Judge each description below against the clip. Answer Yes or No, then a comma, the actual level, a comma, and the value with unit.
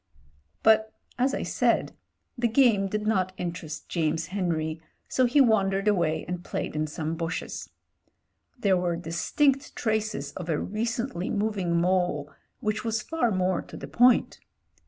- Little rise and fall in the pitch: No, average, 4.6 semitones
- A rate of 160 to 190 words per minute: Yes, average, 170 wpm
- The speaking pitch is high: Yes, high, 195 Hz